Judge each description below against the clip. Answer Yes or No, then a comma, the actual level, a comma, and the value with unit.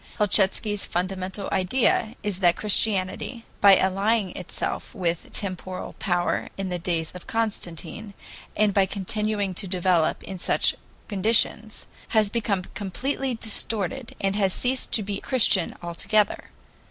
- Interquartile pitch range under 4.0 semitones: Yes, average, 2.8 semitones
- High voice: Yes, high, 200 Hz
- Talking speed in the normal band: No, slow, 130 wpm